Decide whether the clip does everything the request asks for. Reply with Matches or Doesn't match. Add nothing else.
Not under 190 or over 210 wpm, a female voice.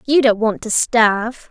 Matches